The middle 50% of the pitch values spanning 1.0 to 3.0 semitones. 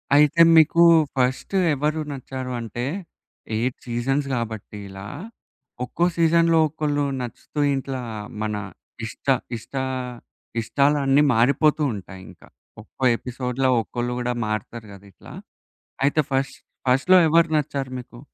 No: average, 3.8 semitones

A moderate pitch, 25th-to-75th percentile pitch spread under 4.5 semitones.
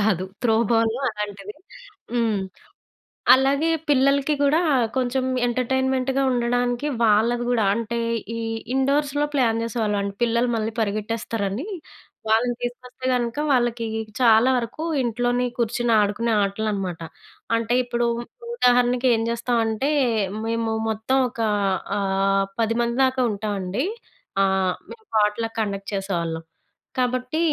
No: high, 230 Hz; average, 3.0 semitones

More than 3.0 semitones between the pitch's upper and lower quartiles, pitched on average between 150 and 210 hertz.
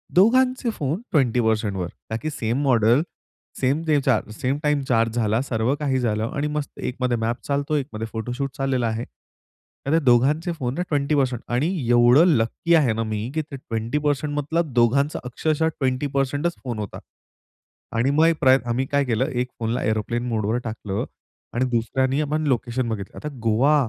No: average, 4.2 semitones; low, 130 Hz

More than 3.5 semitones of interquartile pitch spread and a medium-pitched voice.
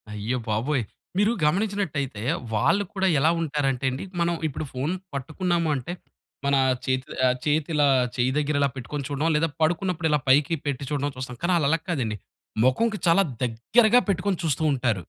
Yes: average, 4.6 semitones; medium, 150 Hz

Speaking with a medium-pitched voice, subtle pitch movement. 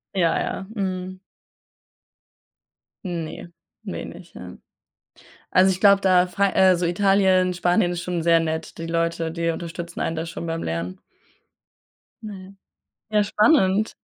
Yes: medium, 180 Hz; narrow, 2.3 semitones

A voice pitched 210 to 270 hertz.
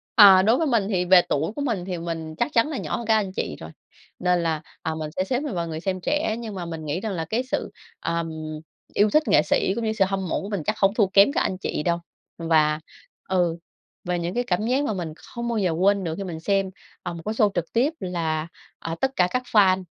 No: high, 190 Hz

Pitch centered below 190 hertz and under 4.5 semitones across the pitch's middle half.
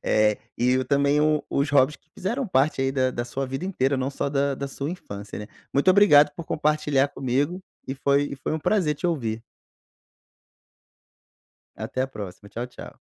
Yes: medium, 140 Hz; average, 2.8 semitones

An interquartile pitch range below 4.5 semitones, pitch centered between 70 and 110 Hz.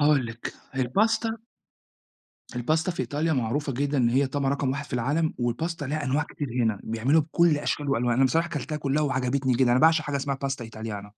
No: average, 3.5 semitones; medium, 140 Hz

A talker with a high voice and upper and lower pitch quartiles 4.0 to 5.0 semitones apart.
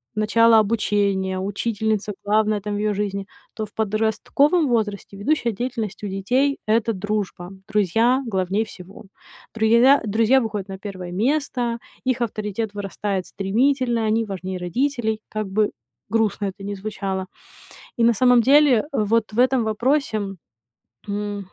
No: high, 215 Hz; narrow, 2.6 semitones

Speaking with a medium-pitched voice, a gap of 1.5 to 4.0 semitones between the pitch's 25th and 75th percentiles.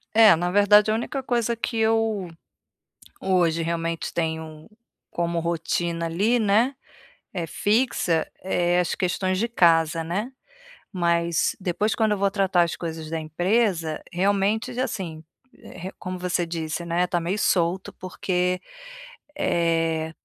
Yes: medium, 180 Hz; average, 3.5 semitones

